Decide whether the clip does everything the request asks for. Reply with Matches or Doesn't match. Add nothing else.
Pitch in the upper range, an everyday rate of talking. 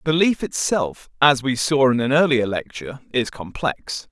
Doesn't match